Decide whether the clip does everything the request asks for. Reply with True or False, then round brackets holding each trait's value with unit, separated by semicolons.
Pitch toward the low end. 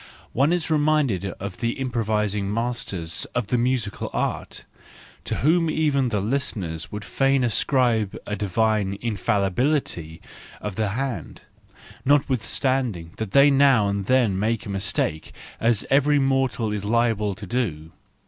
True (115 Hz)